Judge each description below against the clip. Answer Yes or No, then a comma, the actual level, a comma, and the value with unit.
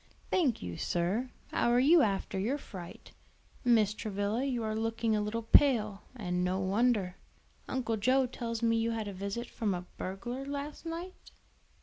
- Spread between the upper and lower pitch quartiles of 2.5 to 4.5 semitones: Yes, average, 3.9 semitones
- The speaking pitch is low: No, high, 225 Hz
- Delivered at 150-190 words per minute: Yes, average, 165 wpm